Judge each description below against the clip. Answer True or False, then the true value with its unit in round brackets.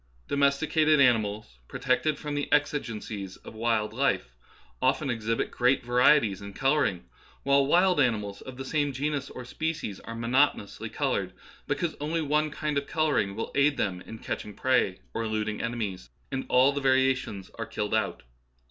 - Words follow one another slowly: False (170 wpm)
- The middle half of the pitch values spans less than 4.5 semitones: False (5.2 semitones)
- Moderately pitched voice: False (130 Hz)